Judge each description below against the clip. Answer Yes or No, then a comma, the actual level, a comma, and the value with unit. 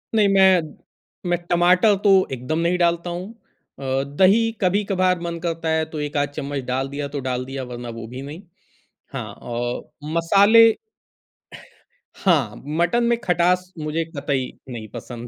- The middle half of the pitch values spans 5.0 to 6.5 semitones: Yes, average, 5.3 semitones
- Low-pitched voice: No, medium, 165 Hz